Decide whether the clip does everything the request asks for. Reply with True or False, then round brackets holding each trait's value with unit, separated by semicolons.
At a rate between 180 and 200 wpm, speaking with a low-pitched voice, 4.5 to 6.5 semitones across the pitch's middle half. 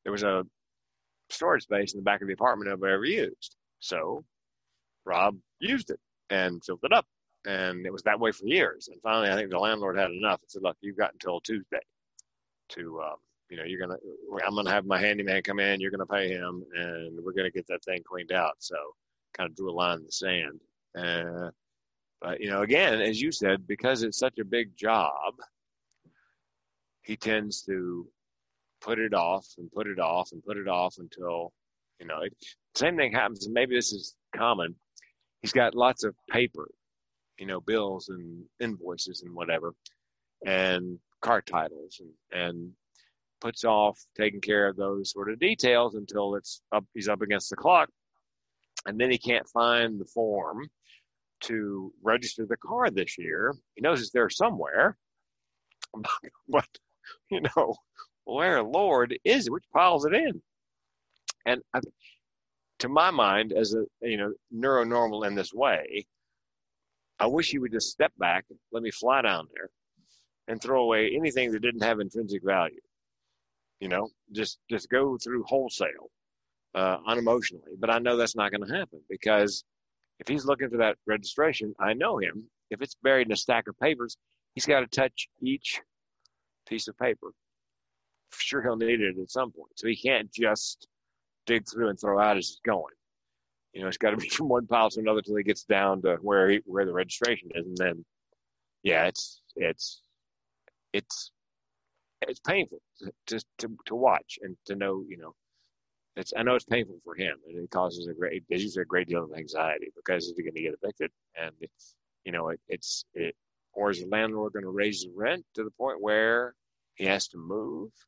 True (185 wpm; 100 Hz; 4.8 semitones)